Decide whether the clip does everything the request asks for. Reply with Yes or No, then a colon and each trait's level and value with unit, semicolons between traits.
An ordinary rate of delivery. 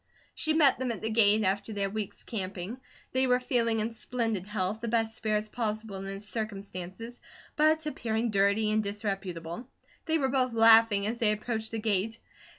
Yes: average, 175 wpm